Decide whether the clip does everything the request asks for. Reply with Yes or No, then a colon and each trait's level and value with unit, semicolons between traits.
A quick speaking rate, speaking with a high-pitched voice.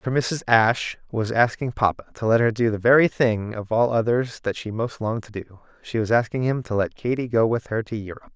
No: fast, 245 wpm; low, 115 Hz